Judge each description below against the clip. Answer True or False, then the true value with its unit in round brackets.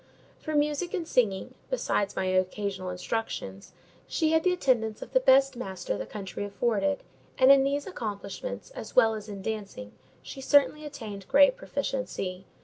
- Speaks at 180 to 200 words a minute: False (155 wpm)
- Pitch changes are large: True (6.4 semitones)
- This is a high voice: True (225 Hz)